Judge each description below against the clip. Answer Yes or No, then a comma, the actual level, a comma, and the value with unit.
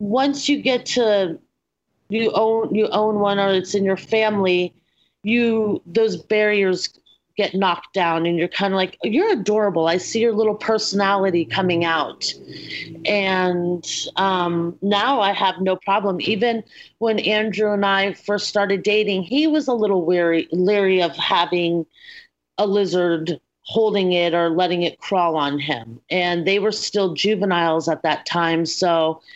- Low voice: No, high, 195 Hz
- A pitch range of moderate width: Yes, average, 3.5 semitones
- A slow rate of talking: No, average, 155 wpm